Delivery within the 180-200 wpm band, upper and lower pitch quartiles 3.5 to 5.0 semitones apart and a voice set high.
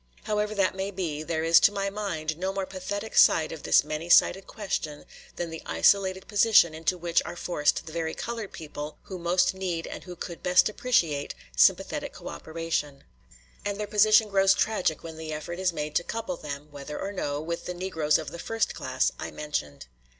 No: average, 195 wpm; average, 4.0 semitones; medium, 175 Hz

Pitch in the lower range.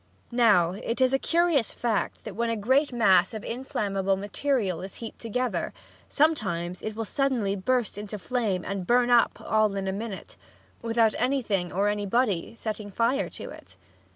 No: high, 220 Hz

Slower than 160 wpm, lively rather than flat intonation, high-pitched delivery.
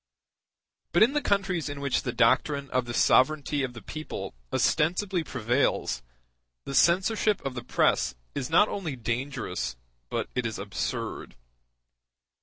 No: average, 140 wpm; wide, 6.0 semitones; medium, 140 Hz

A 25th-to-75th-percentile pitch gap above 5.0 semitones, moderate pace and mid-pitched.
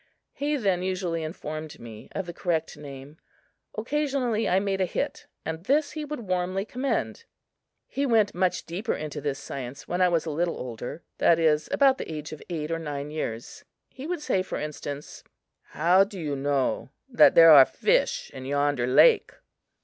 Yes: wide, 5.6 semitones; average, 180 wpm; medium, 170 Hz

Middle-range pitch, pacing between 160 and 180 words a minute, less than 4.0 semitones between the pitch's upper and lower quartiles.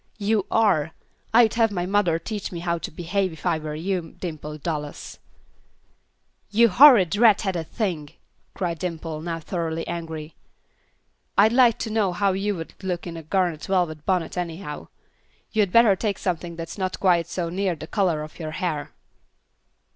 Yes: medium, 180 Hz; average, 165 wpm; average, 3.6 semitones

